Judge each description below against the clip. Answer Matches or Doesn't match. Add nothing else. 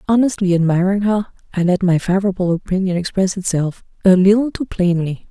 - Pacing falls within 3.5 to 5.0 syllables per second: Doesn't match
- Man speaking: Doesn't match